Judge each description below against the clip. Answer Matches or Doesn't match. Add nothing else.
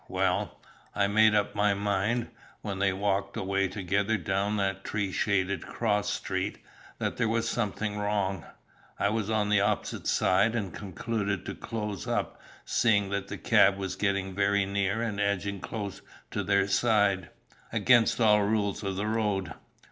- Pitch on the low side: Matches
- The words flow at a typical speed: Matches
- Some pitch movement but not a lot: Doesn't match